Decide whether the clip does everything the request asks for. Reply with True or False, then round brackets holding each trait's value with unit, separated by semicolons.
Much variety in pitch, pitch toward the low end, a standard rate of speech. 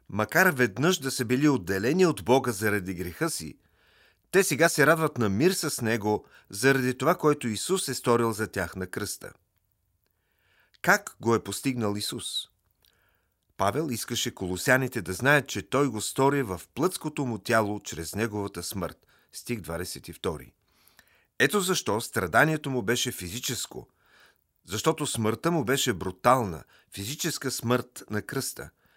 True (5.8 semitones; 120 Hz; 140 wpm)